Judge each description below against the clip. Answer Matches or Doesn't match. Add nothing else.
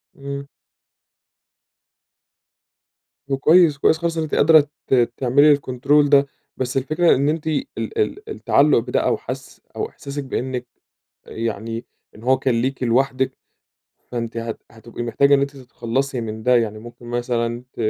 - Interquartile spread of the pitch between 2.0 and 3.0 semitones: Doesn't match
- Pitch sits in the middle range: Doesn't match